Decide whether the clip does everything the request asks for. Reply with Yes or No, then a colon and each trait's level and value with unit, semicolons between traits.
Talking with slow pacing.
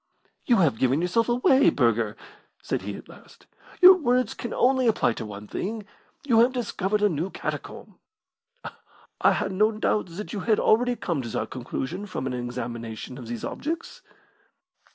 No: average, 170 wpm